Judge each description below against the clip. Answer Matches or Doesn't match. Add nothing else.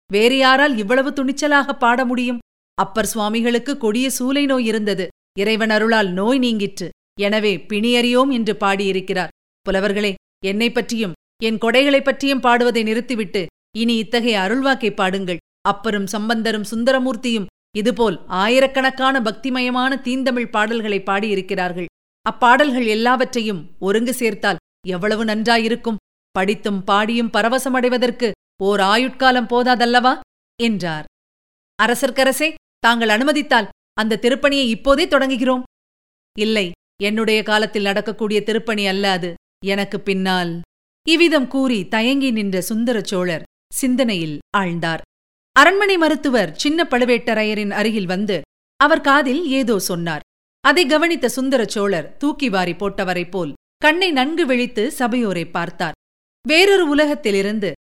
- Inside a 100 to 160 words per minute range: Matches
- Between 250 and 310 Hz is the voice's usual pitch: Doesn't match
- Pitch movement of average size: Matches